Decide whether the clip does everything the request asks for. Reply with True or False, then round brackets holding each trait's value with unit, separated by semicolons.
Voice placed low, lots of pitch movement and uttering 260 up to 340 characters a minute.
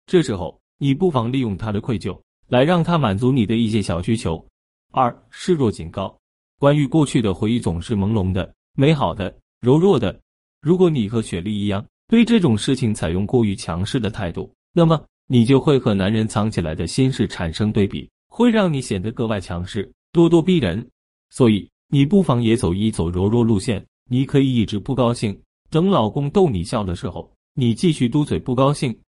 True (115 Hz; 6.0 semitones; 285 characters per minute)